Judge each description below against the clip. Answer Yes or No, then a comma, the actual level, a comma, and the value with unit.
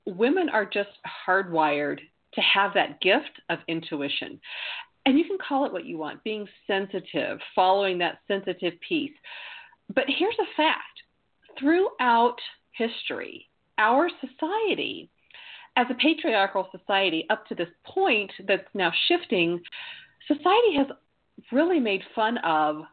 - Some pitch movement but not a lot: No, wide, 8.7 semitones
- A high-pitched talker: Yes, high, 230 Hz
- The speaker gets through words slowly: Yes, slow, 130 wpm